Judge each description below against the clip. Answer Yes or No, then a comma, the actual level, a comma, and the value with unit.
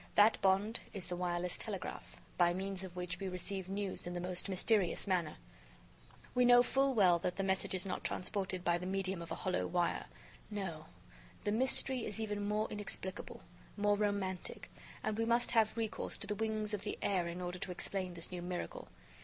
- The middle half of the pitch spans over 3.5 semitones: No, average, 2.7 semitones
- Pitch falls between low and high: No, high, 195 Hz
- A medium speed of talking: Yes, average, 195 wpm